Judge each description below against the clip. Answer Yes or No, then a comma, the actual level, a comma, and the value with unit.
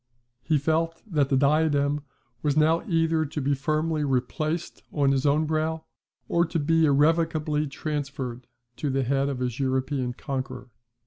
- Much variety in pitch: No, narrow, 2.6 semitones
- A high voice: No, medium, 150 Hz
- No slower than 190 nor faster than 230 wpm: No, average, 150 wpm